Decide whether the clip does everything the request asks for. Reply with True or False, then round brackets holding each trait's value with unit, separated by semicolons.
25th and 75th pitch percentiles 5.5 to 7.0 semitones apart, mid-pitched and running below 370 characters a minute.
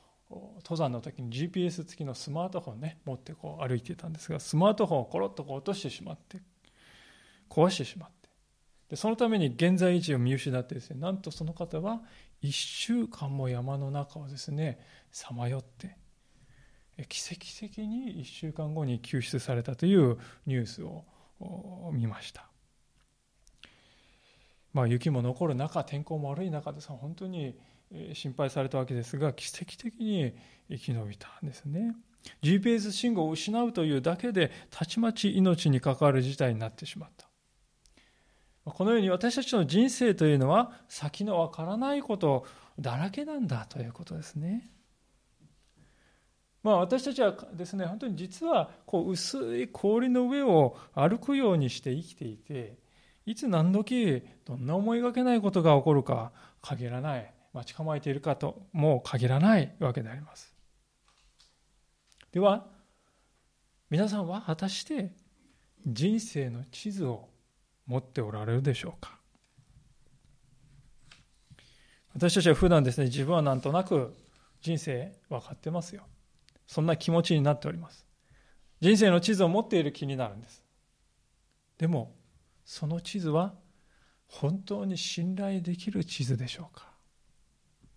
True (5.9 semitones; 160 Hz; 285 characters per minute)